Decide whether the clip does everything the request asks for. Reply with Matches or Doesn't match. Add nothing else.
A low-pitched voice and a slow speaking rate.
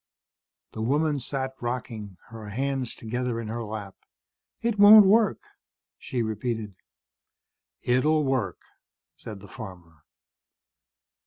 Matches